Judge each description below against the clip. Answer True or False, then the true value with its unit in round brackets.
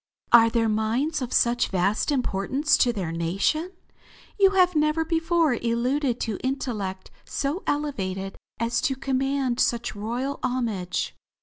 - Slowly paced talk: True (130 wpm)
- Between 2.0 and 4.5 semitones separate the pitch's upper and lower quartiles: False (5.2 semitones)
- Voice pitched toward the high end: True (245 Hz)